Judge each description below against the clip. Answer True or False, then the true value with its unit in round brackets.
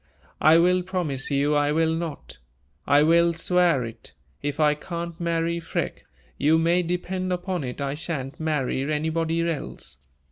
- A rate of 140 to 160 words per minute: True (150 wpm)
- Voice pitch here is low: False (160 Hz)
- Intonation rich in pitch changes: False (2.6 semitones)